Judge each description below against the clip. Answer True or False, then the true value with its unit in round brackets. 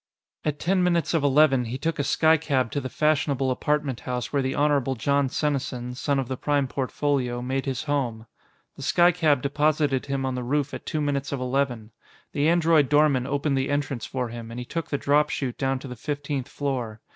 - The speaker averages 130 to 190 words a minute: False (205 wpm)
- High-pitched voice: False (140 Hz)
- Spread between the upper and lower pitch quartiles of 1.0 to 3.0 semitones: True (2.5 semitones)